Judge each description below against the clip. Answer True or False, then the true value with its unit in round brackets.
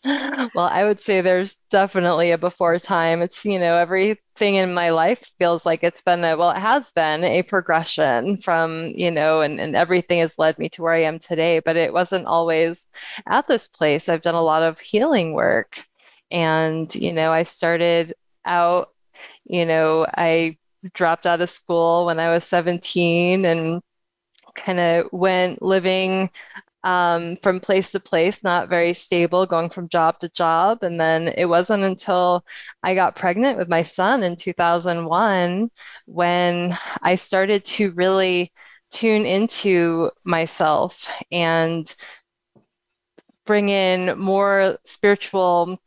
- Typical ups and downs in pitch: False (2.2 semitones)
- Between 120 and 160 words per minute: True (150 wpm)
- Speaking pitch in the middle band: True (175 Hz)